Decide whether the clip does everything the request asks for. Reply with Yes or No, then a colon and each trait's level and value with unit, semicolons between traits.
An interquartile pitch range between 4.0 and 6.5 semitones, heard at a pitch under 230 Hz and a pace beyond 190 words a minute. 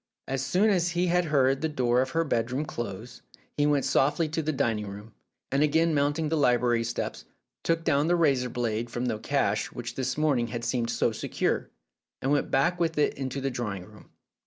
Yes: average, 4.5 semitones; low, 135 Hz; fast, 205 wpm